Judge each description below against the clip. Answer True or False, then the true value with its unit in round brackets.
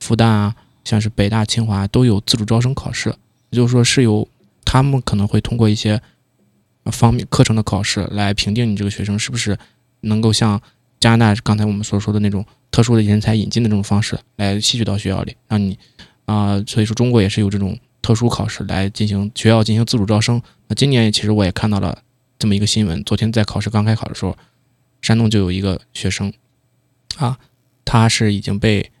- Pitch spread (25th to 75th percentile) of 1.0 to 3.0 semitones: True (2.6 semitones)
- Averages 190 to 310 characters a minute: False (320 characters per minute)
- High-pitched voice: False (110 Hz)